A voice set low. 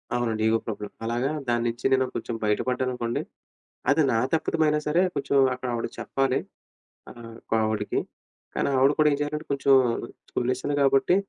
Yes: low, 130 Hz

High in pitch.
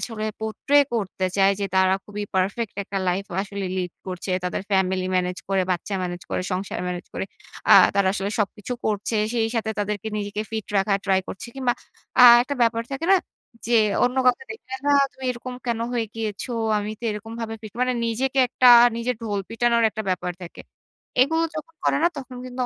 Yes: high, 215 Hz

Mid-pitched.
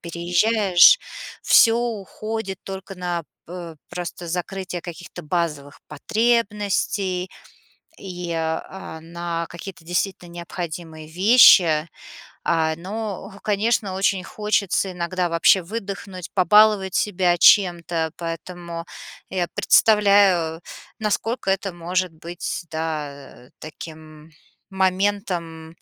Yes: medium, 180 Hz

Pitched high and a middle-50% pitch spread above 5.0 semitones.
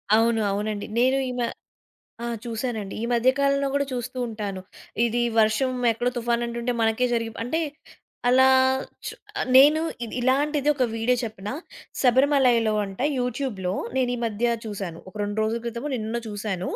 No: high, 235 Hz; average, 2.9 semitones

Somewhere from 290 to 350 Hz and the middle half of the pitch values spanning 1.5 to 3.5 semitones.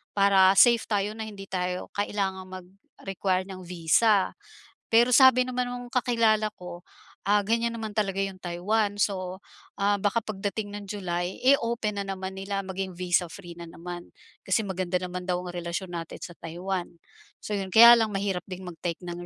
No: high, 195 Hz; average, 2.7 semitones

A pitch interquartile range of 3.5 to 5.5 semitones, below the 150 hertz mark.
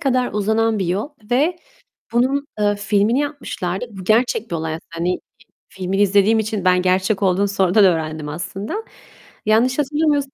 No: average, 4.8 semitones; high, 205 Hz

